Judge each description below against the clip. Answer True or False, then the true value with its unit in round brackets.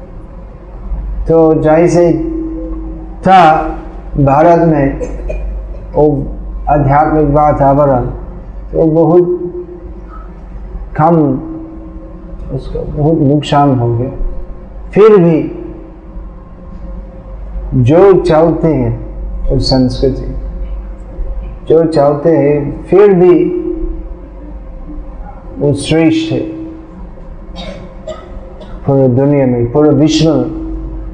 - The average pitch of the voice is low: False (155 Hz)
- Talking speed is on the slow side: True (65 wpm)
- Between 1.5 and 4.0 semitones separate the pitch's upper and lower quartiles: True (3.5 semitones)